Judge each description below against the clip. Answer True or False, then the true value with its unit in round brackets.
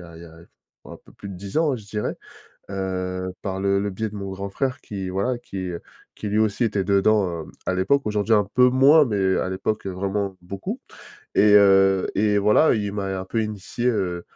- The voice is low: True (100 Hz)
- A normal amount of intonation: False (2.2 semitones)